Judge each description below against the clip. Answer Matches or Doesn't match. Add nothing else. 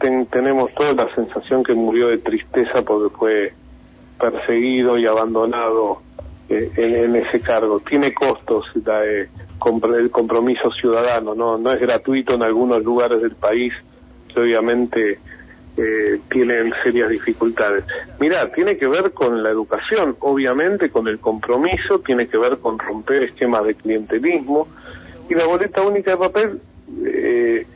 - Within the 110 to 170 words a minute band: Matches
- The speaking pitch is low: Matches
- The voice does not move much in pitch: Doesn't match